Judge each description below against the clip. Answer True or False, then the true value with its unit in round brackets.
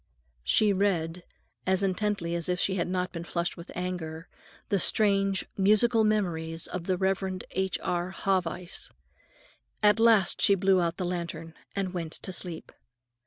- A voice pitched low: False (185 Hz)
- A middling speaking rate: True (155 wpm)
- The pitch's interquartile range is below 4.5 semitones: True (2.4 semitones)